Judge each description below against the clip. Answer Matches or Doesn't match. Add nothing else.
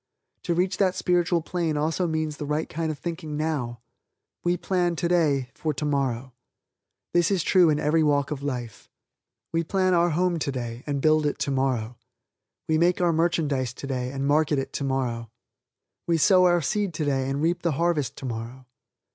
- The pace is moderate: Matches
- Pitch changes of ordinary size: Matches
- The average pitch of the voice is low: Doesn't match